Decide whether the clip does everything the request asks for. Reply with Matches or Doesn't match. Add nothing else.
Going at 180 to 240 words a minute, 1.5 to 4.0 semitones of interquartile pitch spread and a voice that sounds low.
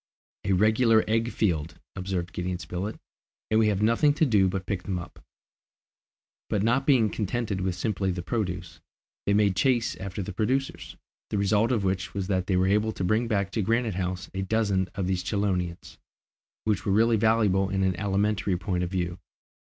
Matches